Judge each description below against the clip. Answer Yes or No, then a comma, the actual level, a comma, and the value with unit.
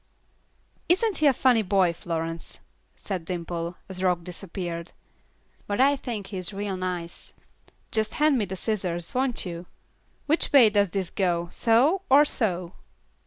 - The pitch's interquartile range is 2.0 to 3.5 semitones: No, wide, 5.5 semitones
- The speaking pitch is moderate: No, high, 195 Hz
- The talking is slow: No, average, 150 wpm